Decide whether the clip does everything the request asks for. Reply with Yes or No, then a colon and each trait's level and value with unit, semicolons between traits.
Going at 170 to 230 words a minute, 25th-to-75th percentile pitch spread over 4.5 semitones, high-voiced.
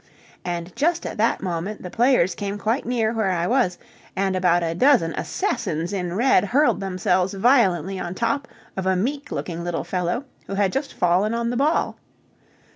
Yes: average, 180 wpm; average, 5.0 semitones; high, 195 Hz